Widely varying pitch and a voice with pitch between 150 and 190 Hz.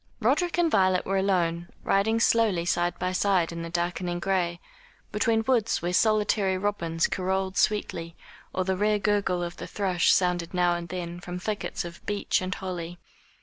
No: average, 2.8 semitones; medium, 185 Hz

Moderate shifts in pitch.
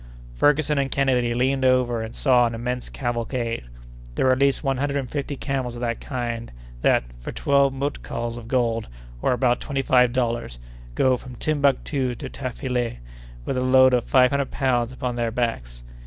No: narrow, 2.3 semitones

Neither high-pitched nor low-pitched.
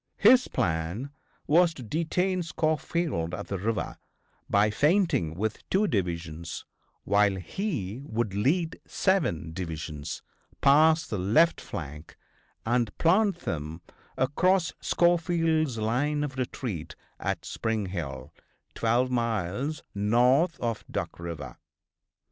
No: low, 120 Hz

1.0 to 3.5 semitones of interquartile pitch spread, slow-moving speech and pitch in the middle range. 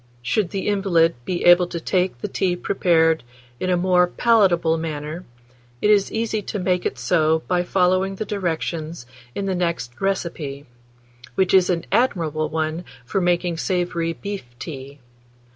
No: average, 2.8 semitones; average, 155 wpm; medium, 175 Hz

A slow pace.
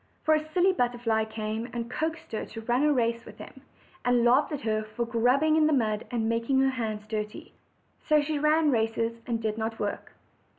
No: fast, 205 wpm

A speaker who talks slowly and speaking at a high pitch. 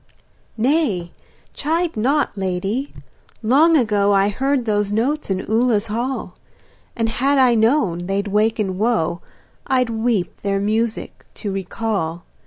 Yes: slow, 125 wpm; high, 220 Hz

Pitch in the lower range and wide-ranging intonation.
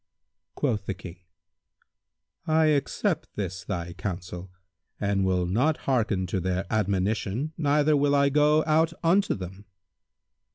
Yes: low, 105 Hz; wide, 8.1 semitones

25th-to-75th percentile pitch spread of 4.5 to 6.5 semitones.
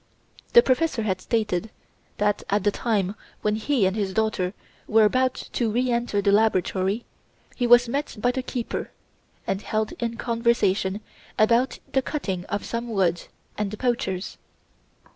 No: average, 3.3 semitones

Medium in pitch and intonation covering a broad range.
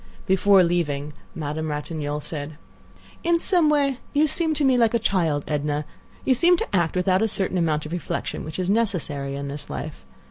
Yes: medium, 175 Hz; wide, 7.6 semitones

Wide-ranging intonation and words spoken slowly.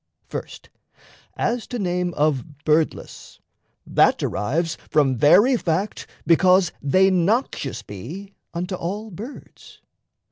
No: average, 4.4 semitones; slow, 105 wpm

